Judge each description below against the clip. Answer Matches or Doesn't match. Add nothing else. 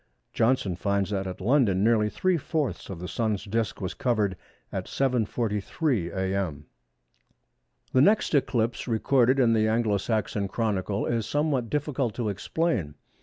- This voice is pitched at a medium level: Doesn't match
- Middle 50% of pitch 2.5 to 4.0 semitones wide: Doesn't match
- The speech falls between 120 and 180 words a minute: Matches